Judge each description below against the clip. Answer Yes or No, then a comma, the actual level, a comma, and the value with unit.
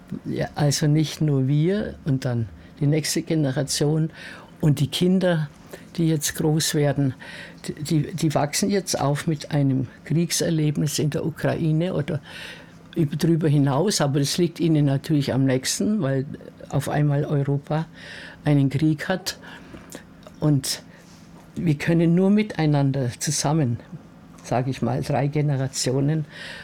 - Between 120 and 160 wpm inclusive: Yes, slow, 125 wpm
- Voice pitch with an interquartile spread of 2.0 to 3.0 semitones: Yes, average, 2.7 semitones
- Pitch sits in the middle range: Yes, medium, 150 Hz